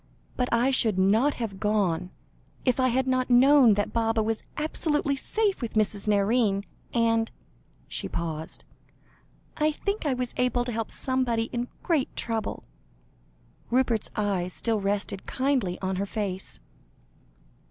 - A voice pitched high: Yes, high, 230 Hz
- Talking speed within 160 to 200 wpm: No, average, 140 wpm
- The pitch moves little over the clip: No, average, 4.1 semitones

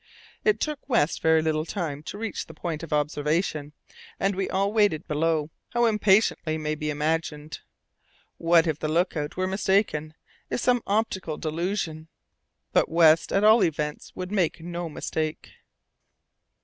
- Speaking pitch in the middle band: Yes, medium, 165 Hz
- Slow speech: No, average, 150 wpm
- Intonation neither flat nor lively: Yes, average, 4.1 semitones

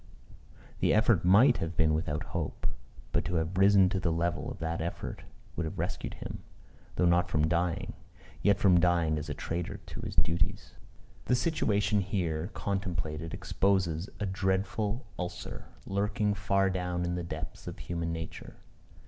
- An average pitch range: Yes, average, 3.1 semitones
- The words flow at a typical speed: Yes, average, 160 wpm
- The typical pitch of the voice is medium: No, very low, 90 Hz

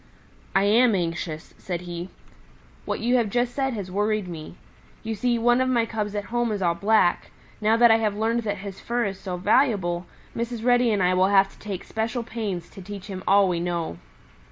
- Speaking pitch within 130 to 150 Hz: No, high, 205 Hz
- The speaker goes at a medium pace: No, fast, 210 wpm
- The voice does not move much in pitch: No, average, 4.0 semitones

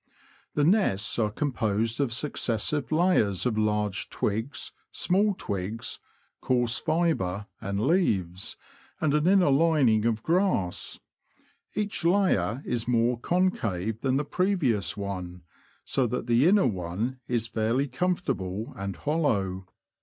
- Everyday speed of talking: No, slow, 125 wpm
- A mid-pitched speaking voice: No, low, 120 Hz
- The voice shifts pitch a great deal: Yes, wide, 7.3 semitones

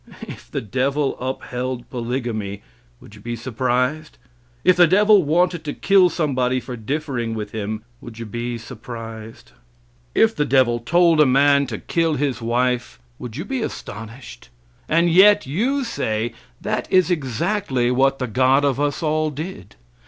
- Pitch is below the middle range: Yes, low, 130 Hz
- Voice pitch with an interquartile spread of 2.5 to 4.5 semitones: No, average, 4.9 semitones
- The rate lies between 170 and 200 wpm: No, average, 155 wpm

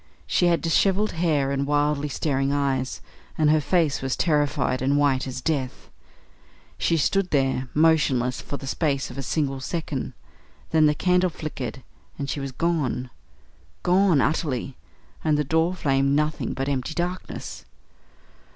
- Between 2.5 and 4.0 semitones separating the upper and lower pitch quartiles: Yes, average, 3.2 semitones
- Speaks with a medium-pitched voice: Yes, medium, 145 Hz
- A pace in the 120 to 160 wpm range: Yes, average, 150 wpm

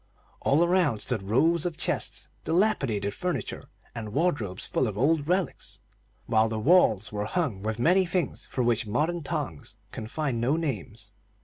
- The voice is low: Yes, low, 130 Hz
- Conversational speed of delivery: Yes, average, 155 wpm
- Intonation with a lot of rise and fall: Yes, wide, 7.4 semitones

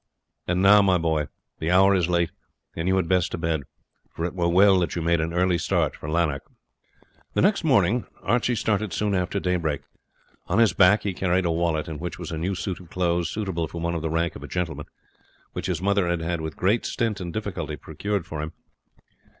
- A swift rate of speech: Yes, fast, 215 wpm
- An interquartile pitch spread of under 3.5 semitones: Yes, average, 2.8 semitones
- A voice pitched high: No, very low, 90 Hz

